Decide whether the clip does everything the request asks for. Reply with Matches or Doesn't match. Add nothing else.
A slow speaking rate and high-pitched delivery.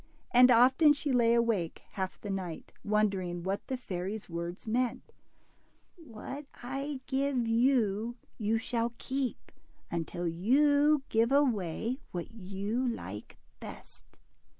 Matches